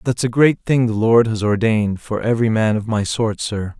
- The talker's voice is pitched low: Yes, low, 110 Hz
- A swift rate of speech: Yes, fast, 235 wpm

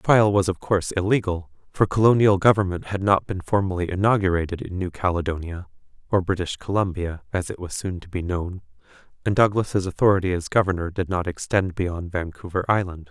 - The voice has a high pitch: No, very low, 95 Hz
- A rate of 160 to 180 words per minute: Yes, average, 175 wpm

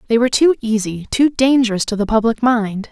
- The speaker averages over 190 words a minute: Yes, fast, 205 wpm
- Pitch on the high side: Yes, high, 230 Hz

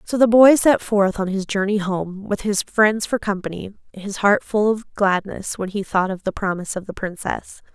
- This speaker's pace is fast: Yes, fast, 215 wpm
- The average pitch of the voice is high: Yes, high, 200 Hz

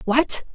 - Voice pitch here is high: Yes, very high, 260 Hz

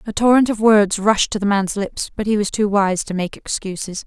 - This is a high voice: Yes, high, 205 Hz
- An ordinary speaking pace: No, fast, 250 wpm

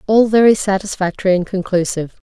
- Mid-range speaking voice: No, high, 195 Hz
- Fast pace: No, slow, 130 wpm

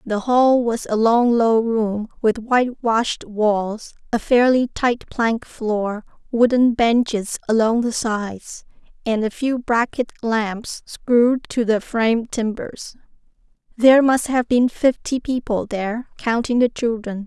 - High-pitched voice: Yes, high, 230 Hz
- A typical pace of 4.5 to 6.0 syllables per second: No, 3.9 syllables/s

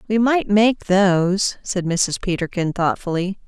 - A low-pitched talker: No, high, 190 Hz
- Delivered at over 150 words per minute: No, average, 140 wpm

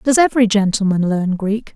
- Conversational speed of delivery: Yes, average, 170 wpm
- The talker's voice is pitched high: Yes, high, 210 Hz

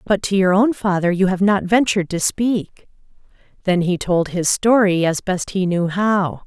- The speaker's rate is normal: Yes, average, 195 wpm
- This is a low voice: No, high, 190 Hz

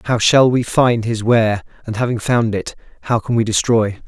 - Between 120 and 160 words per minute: No, fast, 205 wpm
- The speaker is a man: Yes, male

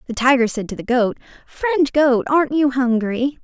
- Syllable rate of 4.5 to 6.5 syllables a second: Yes, 4.7 syllables/s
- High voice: Yes, very high, 260 Hz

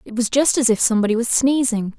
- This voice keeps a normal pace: No, fast, 240 wpm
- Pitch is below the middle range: No, high, 235 Hz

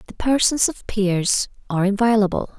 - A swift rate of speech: No, average, 140 wpm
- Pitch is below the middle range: No, high, 210 Hz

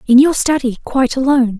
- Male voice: No, female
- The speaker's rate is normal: Yes, average, 190 wpm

